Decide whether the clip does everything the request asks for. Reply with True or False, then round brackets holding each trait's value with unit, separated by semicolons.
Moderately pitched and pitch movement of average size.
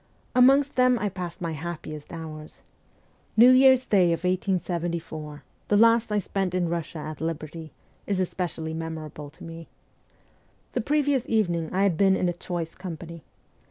True (175 Hz; 4.2 semitones)